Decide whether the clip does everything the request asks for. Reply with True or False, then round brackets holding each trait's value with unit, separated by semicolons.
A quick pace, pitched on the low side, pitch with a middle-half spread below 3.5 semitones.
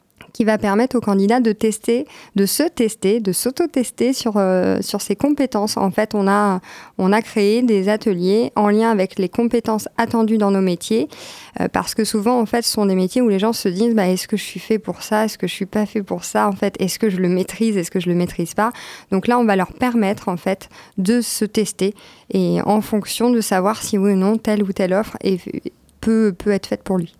False (245 wpm; 210 Hz; 2.8 semitones)